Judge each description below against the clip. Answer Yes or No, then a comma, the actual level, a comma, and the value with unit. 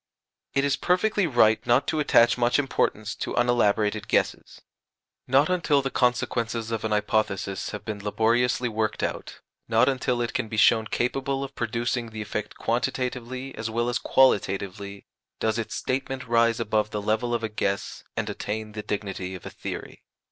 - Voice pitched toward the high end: No, low, 115 Hz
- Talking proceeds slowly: No, average, 170 wpm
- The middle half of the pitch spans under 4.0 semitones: Yes, average, 2.9 semitones